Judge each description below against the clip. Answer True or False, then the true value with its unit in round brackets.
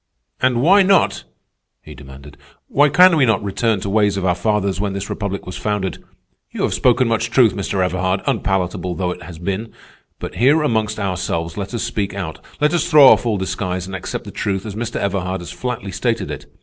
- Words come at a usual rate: False (210 wpm)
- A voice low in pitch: True (100 Hz)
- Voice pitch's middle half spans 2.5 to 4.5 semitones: True (4.2 semitones)